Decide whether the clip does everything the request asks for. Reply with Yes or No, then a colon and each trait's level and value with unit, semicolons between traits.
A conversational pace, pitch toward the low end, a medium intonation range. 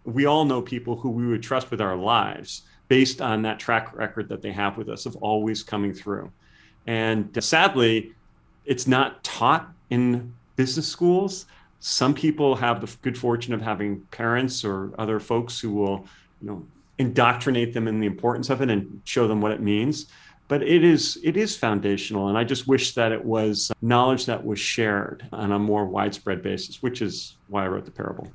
Yes: average, 195 wpm; low, 115 Hz; average, 3.6 semitones